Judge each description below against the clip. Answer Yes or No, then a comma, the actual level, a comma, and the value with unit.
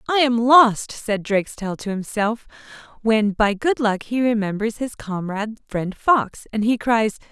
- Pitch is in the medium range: No, high, 220 Hz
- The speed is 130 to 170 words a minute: Yes, average, 165 wpm